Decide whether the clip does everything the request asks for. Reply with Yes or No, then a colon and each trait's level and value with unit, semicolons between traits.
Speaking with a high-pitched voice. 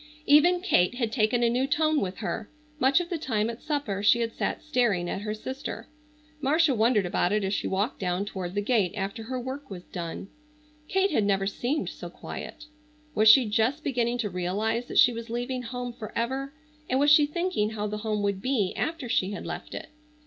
Yes: high, 230 Hz